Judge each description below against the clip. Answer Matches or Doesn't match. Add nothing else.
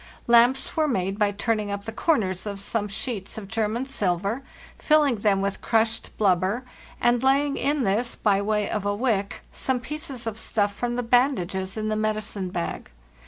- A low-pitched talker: Doesn't match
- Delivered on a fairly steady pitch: Doesn't match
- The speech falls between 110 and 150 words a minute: Doesn't match